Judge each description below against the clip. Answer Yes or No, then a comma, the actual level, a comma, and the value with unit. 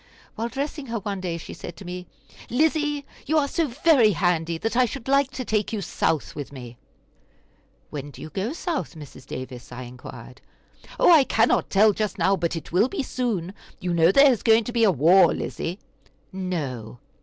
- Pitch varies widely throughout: Yes, wide, 7.5 semitones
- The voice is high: Yes, high, 200 Hz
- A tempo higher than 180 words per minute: Yes, average, 190 wpm